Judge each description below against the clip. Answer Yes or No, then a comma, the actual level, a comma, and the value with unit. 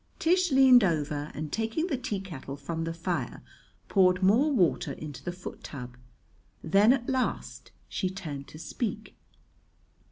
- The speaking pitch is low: No, medium, 185 Hz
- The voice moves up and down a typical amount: No, wide, 7.7 semitones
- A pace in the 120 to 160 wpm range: Yes, average, 140 wpm